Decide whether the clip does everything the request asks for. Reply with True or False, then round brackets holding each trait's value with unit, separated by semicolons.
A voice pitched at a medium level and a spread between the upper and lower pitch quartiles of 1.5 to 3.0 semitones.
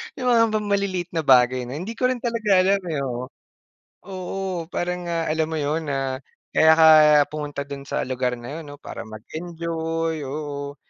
False (160 Hz; 4.1 semitones)